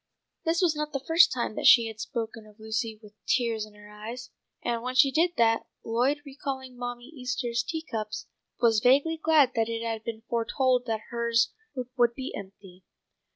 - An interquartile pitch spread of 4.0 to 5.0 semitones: No, average, 3.0 semitones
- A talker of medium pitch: No, high, 235 Hz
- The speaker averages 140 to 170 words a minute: No, average, 185 wpm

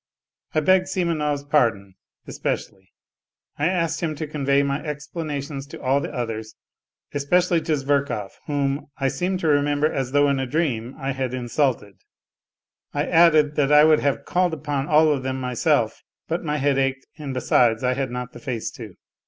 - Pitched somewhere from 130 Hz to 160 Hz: Yes, medium, 140 Hz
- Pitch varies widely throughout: No, average, 2.7 semitones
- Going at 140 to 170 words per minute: No, average, 180 wpm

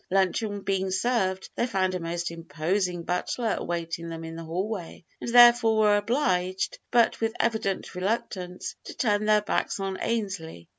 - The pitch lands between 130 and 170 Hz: No, high, 190 Hz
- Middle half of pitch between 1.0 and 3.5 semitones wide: No, average, 3.9 semitones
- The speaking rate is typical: Yes, average, 155 wpm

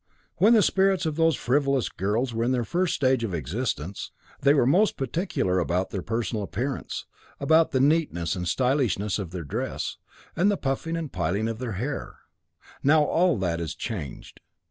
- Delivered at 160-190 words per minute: Yes, average, 180 wpm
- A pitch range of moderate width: No, wide, 8.0 semitones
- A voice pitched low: Yes, low, 125 Hz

